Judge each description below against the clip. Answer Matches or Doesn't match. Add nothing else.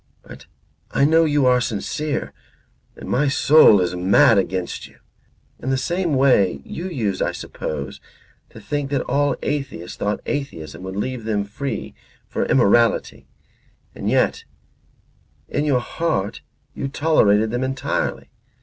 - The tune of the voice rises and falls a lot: Matches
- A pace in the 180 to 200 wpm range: Doesn't match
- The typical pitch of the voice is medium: Doesn't match